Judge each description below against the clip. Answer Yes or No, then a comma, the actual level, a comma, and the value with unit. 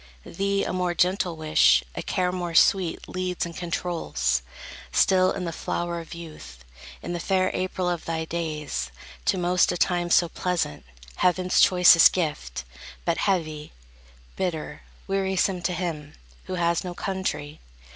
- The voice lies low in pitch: No, medium, 175 Hz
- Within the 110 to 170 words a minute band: Yes, average, 145 wpm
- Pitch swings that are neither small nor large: No, narrow, 2.3 semitones